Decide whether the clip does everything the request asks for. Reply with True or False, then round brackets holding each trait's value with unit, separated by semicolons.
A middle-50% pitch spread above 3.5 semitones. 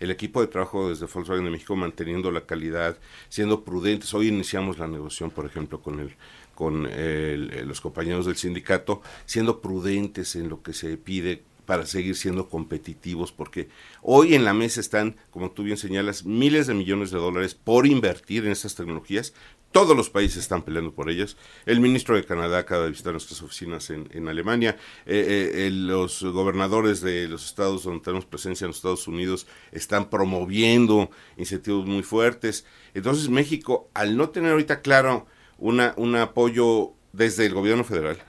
True (4.1 semitones)